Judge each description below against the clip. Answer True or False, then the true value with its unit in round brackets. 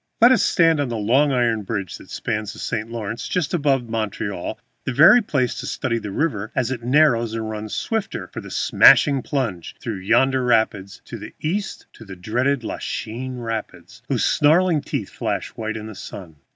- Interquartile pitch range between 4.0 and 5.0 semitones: True (4.5 semitones)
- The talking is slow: False (185 wpm)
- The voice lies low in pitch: True (115 Hz)